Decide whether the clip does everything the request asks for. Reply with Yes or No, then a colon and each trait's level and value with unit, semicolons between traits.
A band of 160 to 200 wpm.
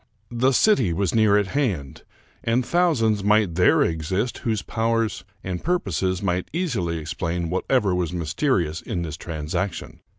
No: average, 140 wpm